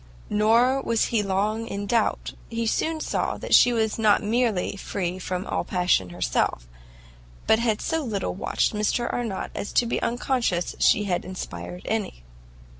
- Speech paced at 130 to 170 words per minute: Yes, average, 165 wpm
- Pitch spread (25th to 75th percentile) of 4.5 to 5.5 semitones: No, average, 3.8 semitones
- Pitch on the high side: Yes, high, 215 Hz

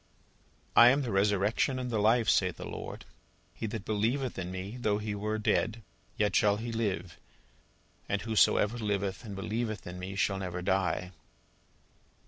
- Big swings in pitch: No, average, 2.8 semitones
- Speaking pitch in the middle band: No, low, 105 Hz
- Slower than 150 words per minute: No, average, 160 wpm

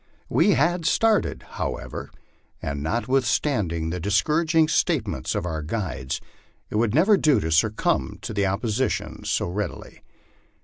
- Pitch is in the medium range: No, low, 110 Hz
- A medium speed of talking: No, slow, 125 wpm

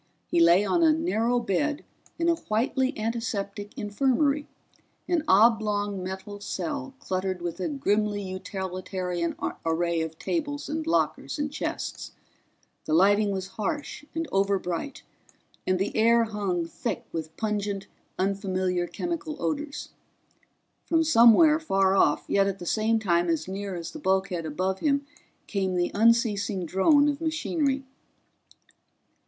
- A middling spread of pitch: No, wide, 6.9 semitones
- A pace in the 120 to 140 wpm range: Yes, slow, 135 wpm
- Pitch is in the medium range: No, high, 205 Hz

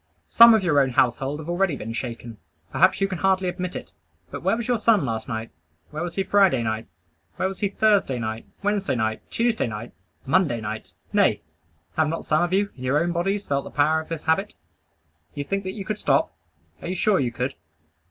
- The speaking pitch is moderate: Yes, medium, 165 Hz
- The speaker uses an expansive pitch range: Yes, wide, 7.5 semitones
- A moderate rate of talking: No, fast, 215 wpm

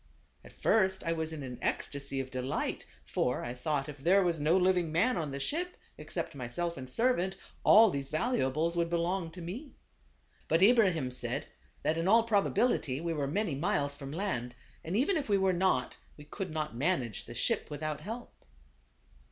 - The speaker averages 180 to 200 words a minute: Yes, average, 185 wpm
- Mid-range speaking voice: Yes, medium, 165 Hz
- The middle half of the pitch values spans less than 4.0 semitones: No, average, 5.3 semitones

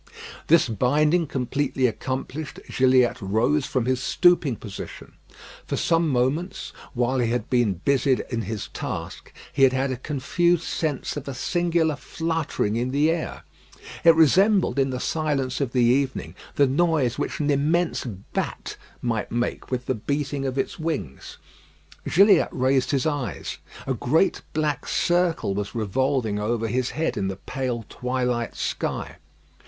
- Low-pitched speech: Yes, low, 130 Hz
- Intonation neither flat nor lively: Yes, average, 4.1 semitones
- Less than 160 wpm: Yes, average, 150 wpm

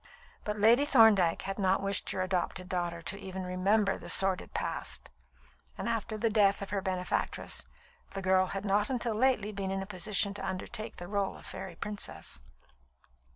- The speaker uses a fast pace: No, average, 175 wpm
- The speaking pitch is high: Yes, high, 195 Hz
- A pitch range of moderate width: No, narrow, 2.2 semitones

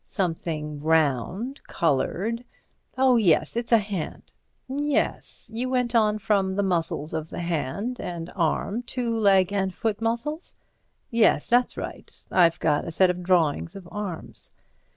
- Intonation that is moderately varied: No, wide, 5.9 semitones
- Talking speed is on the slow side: Yes, slow, 130 wpm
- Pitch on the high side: Yes, high, 195 Hz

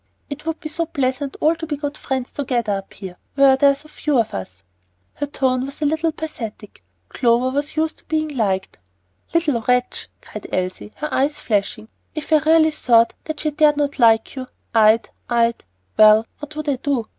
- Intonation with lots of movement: No, average, 4.7 semitones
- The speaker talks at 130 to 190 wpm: No, average, 200 wpm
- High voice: Yes, very high, 275 Hz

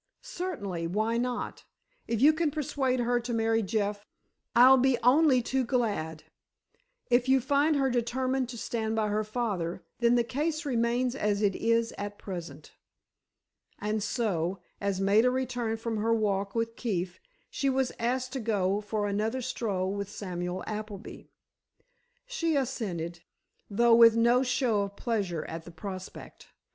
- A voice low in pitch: No, high, 230 Hz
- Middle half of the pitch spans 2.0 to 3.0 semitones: No, average, 3.8 semitones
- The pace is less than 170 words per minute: Yes, average, 150 wpm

